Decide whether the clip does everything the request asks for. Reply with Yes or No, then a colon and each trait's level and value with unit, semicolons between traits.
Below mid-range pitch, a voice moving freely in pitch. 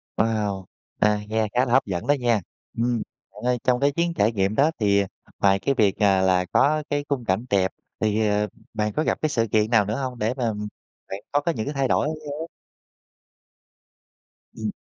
No: low, 110 Hz; average, 4.7 semitones